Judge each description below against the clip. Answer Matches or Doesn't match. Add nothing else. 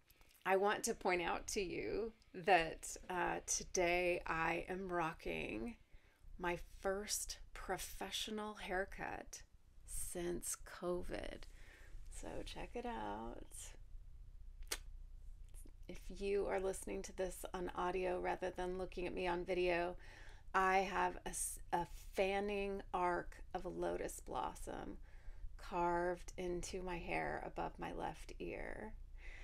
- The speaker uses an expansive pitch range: Matches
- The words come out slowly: Matches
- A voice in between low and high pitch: Matches